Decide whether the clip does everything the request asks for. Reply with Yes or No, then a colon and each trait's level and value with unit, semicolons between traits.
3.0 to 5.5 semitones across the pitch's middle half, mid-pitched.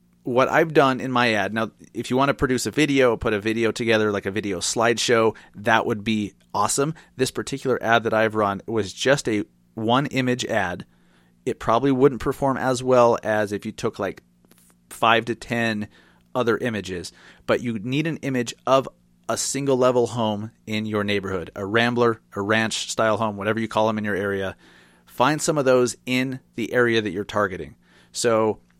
No: average, 3.4 semitones; low, 115 Hz